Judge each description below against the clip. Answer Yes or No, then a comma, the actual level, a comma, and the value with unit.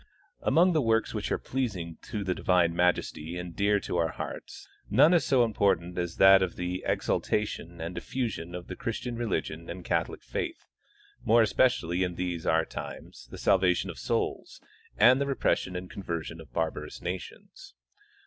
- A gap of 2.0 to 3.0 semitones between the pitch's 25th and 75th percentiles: No, average, 4.7 semitones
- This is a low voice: Yes, very low, 90 Hz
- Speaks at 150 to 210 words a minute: Yes, average, 170 wpm